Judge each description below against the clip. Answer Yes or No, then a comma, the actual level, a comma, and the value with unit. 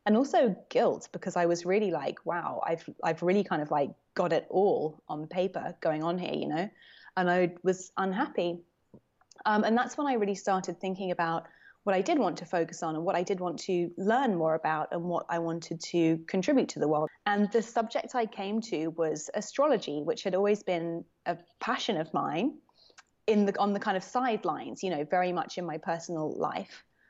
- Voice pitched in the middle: Yes, medium, 180 Hz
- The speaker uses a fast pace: Yes, fast, 210 wpm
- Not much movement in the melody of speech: No, average, 3.8 semitones